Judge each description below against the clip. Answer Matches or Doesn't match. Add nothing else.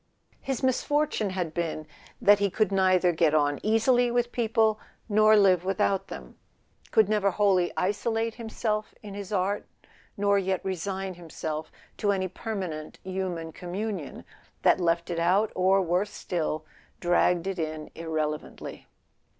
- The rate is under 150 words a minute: Matches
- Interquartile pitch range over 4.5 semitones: Doesn't match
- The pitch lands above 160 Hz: Matches